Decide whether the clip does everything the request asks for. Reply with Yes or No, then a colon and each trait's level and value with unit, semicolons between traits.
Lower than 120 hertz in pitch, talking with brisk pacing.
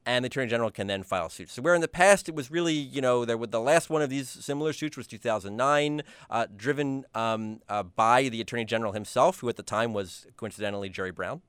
No: low, 125 Hz; fast, 235 wpm